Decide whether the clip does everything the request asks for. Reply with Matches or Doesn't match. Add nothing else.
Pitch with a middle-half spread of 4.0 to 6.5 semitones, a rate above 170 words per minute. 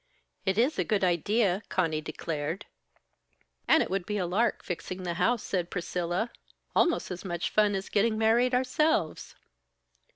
Doesn't match